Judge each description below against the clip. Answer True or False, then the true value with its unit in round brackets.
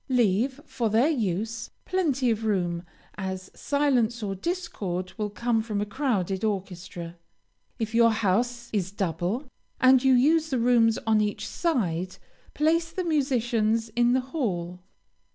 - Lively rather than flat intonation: False (4.9 semitones)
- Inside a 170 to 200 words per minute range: False (140 wpm)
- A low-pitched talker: False (225 Hz)